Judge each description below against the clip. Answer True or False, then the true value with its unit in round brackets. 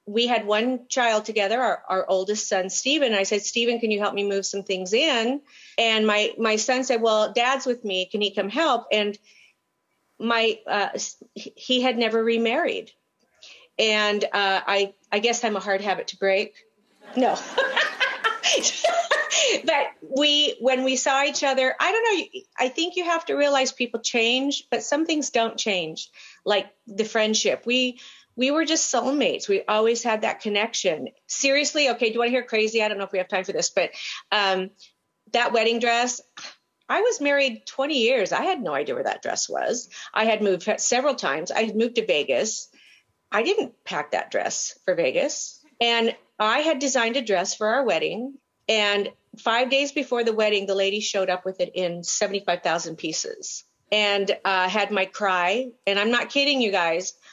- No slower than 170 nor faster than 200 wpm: True (185 wpm)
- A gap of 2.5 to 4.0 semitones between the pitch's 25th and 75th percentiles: False (5.1 semitones)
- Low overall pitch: False (230 Hz)